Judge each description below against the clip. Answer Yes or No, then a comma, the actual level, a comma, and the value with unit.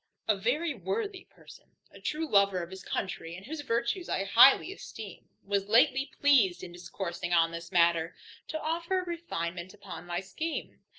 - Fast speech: No, average, 170 wpm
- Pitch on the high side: Yes, high, 200 Hz